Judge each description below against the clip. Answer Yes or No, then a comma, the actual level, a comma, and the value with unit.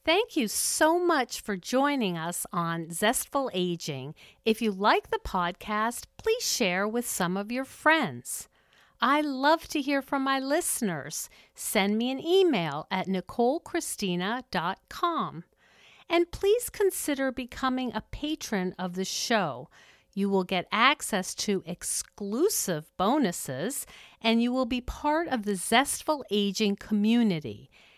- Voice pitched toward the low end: No, high, 230 Hz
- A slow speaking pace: Yes, slow, 130 wpm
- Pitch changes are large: Yes, wide, 7.5 semitones